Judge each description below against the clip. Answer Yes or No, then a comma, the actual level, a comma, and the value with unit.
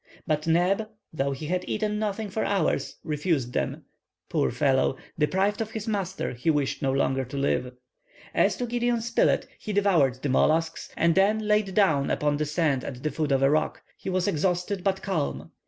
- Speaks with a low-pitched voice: No, medium, 165 Hz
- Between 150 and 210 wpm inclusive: Yes, average, 190 wpm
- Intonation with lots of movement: Yes, wide, 5.9 semitones